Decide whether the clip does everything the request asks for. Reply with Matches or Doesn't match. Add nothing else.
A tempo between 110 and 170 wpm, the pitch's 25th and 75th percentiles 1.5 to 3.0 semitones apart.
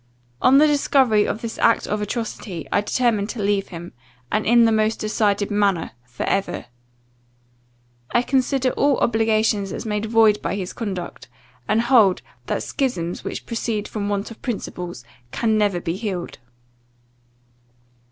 Matches